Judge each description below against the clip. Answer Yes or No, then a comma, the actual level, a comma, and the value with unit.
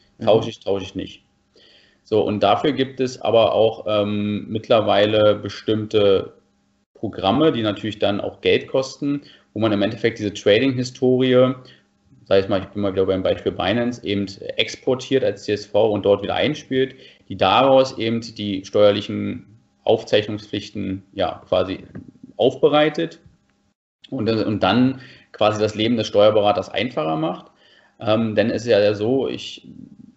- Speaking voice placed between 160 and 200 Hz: No, low, 110 Hz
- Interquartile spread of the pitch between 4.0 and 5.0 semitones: Yes, average, 4.3 semitones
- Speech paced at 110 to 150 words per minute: Yes, average, 145 wpm